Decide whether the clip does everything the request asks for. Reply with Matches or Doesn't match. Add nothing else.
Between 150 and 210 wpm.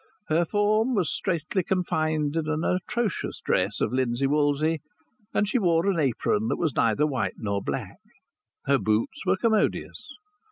Matches